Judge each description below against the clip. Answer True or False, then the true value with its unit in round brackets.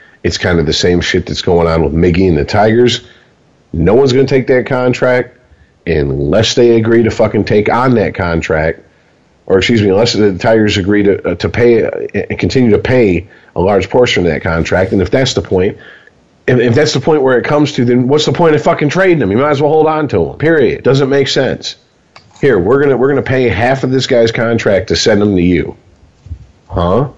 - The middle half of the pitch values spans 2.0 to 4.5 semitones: False (4.9 semitones)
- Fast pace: True (230 wpm)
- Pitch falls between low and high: False (120 Hz)